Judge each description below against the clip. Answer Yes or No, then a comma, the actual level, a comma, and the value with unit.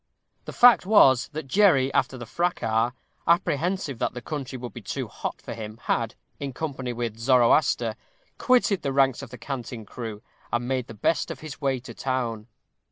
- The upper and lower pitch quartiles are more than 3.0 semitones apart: Yes, average, 3.7 semitones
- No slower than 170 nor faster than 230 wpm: Yes, average, 180 wpm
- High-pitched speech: No, low, 130 Hz